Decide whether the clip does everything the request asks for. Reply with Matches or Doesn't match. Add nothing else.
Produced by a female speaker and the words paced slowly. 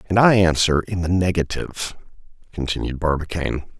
Doesn't match